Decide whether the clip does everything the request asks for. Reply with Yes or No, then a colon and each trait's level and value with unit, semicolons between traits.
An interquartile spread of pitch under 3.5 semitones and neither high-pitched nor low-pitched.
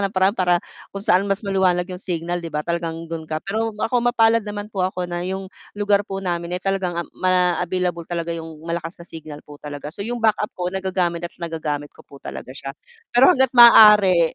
Yes: average, 2.9 semitones; medium, 180 Hz